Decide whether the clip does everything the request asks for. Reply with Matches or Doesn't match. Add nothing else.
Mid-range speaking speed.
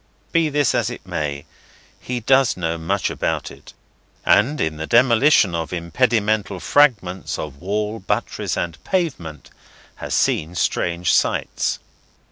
Doesn't match